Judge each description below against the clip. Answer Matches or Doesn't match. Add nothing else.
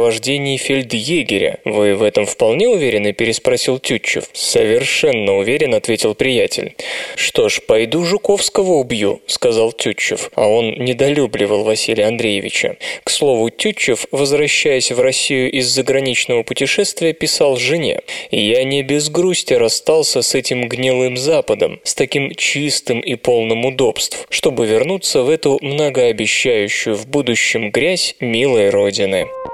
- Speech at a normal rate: Matches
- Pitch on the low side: Doesn't match